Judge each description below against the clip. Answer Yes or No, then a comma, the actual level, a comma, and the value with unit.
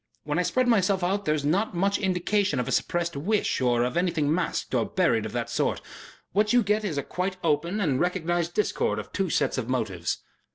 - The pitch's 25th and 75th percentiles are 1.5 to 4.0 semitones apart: No, average, 5.1 semitones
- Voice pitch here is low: No, medium, 175 Hz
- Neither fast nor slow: No, fast, 215 wpm